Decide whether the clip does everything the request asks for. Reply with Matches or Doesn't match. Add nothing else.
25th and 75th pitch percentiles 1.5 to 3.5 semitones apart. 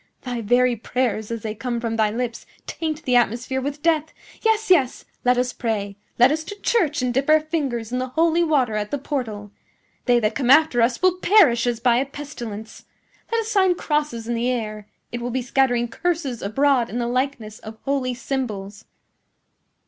Doesn't match